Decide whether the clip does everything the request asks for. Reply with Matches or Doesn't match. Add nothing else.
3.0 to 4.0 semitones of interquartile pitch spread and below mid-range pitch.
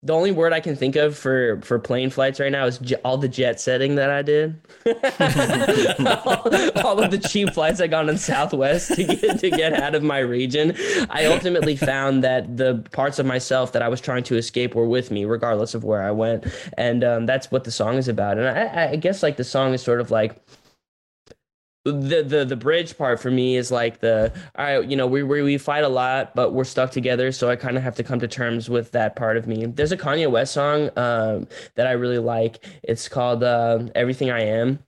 Matches